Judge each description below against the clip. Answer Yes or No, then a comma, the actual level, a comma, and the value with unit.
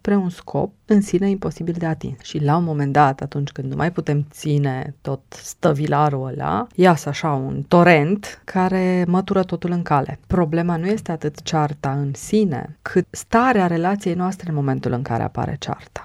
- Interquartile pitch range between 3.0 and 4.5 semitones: Yes, average, 4.1 semitones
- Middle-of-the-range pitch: Yes, medium, 165 Hz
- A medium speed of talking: No, fast, 180 wpm